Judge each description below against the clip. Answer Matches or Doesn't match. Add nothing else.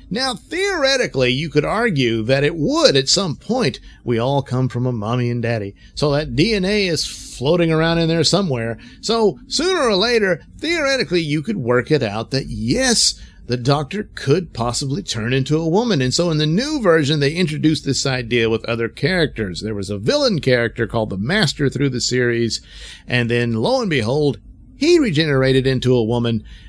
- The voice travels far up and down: Matches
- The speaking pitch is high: Doesn't match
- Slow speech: Doesn't match